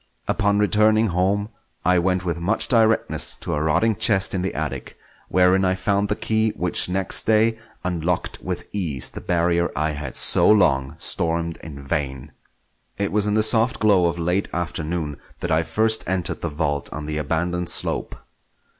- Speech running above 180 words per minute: No, average, 170 wpm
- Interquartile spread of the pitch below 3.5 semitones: No, average, 4.2 semitones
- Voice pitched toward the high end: No, very low, 90 Hz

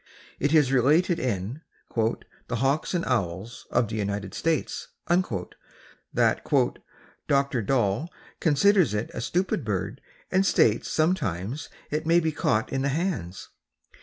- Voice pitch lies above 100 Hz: Yes, low, 135 Hz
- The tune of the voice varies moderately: No, wide, 7.1 semitones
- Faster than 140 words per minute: No, slow, 135 wpm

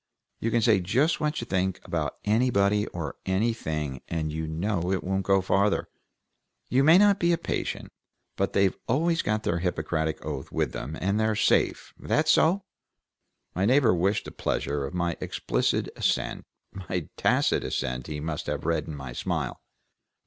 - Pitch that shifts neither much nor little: No, wide, 6.3 semitones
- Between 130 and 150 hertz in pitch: No, very low, 95 Hz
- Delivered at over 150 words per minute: Yes, average, 170 wpm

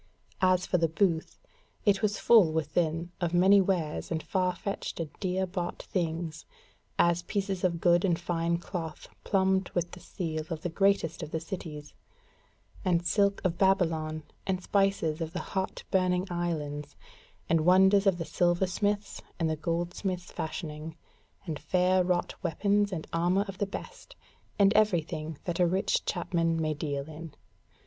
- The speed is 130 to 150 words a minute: No, average, 160 wpm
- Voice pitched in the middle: Yes, medium, 175 Hz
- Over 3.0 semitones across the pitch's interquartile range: No, average, 2.7 semitones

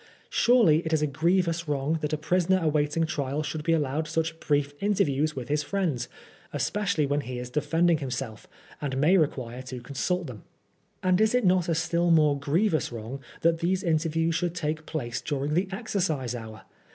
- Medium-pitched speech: Yes, medium, 155 Hz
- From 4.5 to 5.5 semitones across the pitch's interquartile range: No, average, 3.4 semitones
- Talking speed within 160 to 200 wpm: Yes, average, 185 wpm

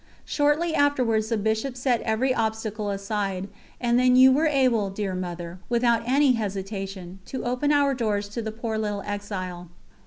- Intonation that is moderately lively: Yes, average, 4.1 semitones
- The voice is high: Yes, high, 220 Hz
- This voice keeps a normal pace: Yes, average, 160 wpm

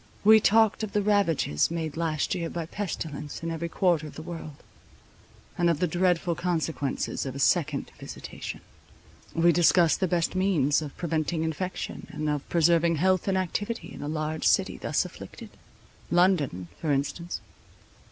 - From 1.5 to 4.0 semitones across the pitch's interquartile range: Yes, average, 2.8 semitones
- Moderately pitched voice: Yes, medium, 165 Hz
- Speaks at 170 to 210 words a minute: No, average, 155 wpm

